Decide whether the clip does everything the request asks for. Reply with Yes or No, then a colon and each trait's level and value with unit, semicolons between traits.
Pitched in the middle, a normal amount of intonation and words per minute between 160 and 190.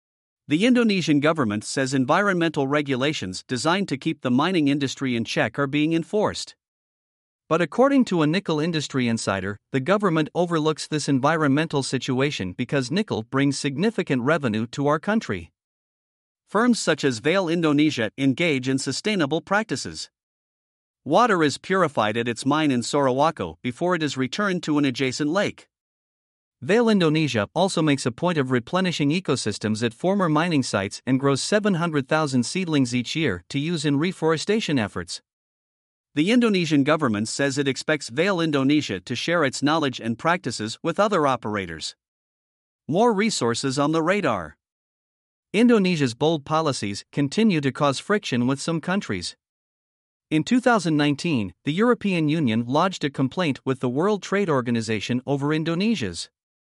No: medium, 150 Hz; average, 4.8 semitones; average, 140 wpm